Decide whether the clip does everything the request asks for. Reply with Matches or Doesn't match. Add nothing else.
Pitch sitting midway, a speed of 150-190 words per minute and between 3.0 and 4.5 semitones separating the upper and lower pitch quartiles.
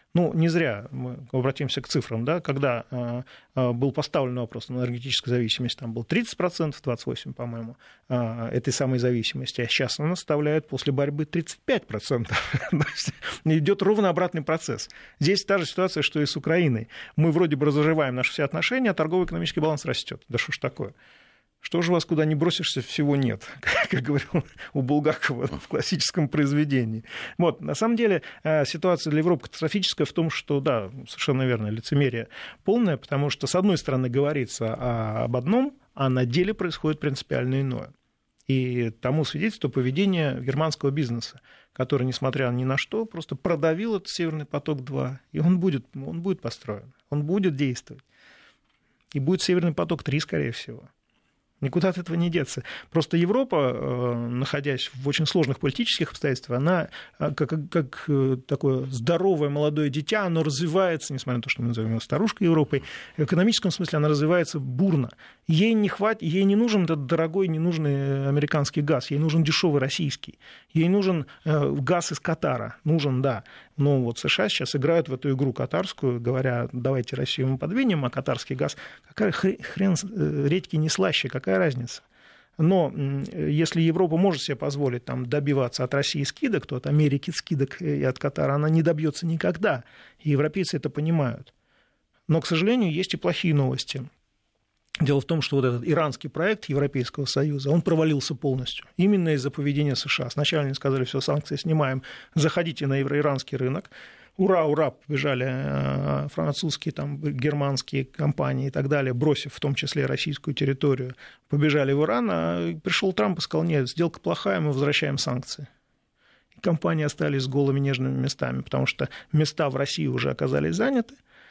Matches